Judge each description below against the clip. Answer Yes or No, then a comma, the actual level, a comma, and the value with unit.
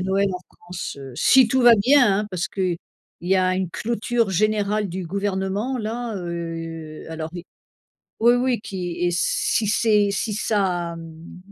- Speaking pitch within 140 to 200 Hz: Yes, high, 190 Hz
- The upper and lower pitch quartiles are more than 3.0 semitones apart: Yes, average, 3.7 semitones